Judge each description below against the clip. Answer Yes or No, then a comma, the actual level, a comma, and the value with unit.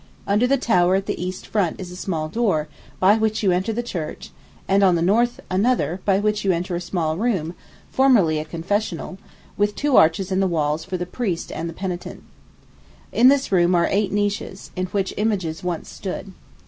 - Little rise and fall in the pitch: No, average, 3.2 semitones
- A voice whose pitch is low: No, high, 190 Hz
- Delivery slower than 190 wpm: No, average, 200 wpm